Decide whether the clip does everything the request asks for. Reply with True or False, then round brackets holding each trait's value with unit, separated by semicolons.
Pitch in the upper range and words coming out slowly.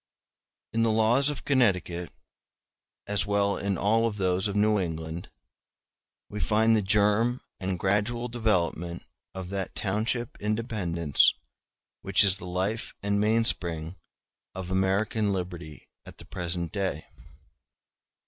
False (100 Hz; 130 wpm)